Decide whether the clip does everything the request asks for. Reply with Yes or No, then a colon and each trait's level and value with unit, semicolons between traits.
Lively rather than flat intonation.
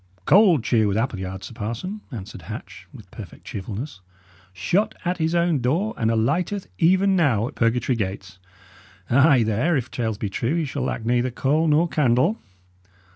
Yes: wide, 7.0 semitones